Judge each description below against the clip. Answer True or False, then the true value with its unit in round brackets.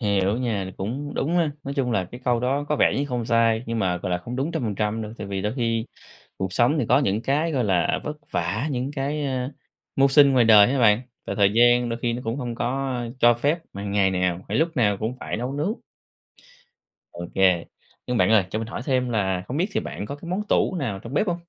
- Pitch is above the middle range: False (120 Hz)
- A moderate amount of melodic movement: True (4.7 semitones)